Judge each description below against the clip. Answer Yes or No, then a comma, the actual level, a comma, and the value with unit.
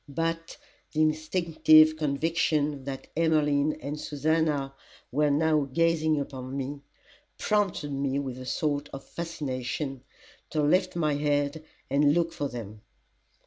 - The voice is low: No, medium, 150 Hz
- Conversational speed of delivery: No, slow, 125 wpm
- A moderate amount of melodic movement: No, narrow, 2.3 semitones